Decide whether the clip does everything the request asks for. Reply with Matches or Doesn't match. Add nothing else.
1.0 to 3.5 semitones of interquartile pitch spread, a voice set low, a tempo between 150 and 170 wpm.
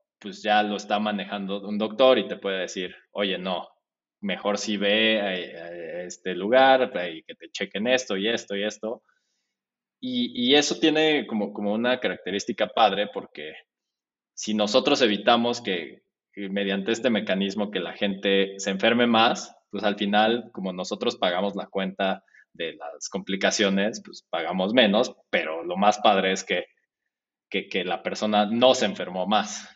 Matches